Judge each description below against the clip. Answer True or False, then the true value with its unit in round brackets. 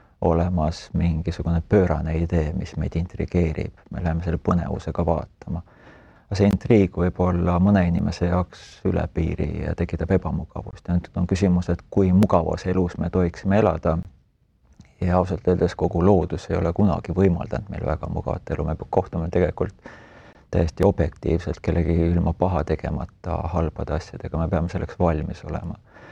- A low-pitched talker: True (90 Hz)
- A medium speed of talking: True (145 wpm)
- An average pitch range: False (2.1 semitones)